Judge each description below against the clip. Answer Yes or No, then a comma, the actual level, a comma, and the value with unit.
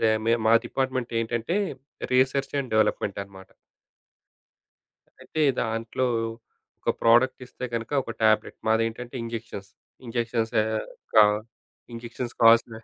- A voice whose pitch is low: Yes, low, 115 Hz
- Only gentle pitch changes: Yes, narrow, 1.8 semitones